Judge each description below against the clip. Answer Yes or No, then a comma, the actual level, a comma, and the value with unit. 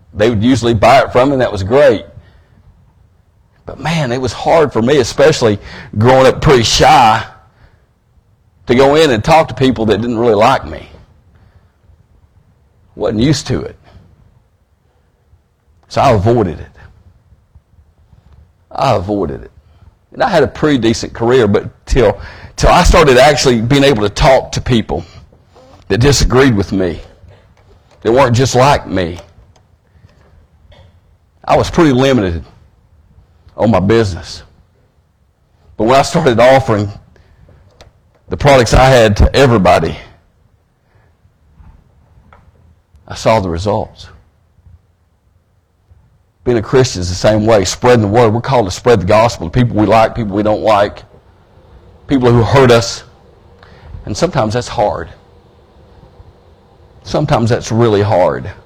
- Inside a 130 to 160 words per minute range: Yes, slow, 135 wpm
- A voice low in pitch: Yes, low, 100 Hz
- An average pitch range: Yes, average, 4.8 semitones